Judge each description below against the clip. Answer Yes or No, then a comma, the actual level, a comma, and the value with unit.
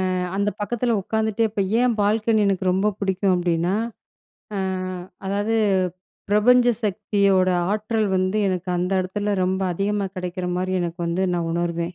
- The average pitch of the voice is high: Yes, high, 195 Hz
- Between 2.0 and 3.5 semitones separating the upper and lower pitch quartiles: Yes, narrow, 2.6 semitones